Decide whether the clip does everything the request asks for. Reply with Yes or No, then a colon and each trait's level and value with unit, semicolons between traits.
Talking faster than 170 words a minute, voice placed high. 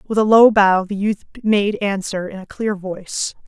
Yes: fast, 205 wpm; high, 200 Hz